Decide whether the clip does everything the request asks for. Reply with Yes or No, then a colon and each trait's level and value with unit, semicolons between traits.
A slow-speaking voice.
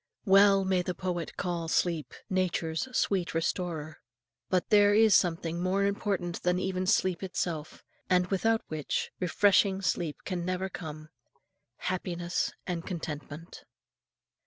Yes: slow, 125 wpm